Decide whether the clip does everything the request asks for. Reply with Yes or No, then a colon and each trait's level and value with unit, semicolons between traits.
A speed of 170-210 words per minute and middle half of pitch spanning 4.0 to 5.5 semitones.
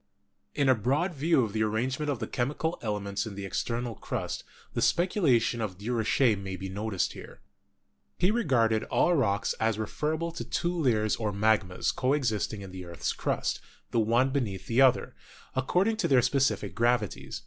Yes: average, 175 wpm; average, 4.7 semitones